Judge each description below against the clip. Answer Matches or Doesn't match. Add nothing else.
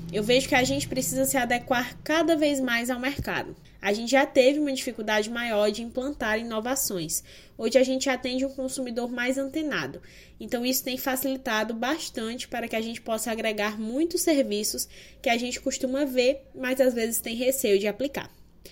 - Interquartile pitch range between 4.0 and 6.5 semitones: Doesn't match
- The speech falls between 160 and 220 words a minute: Matches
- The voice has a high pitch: Matches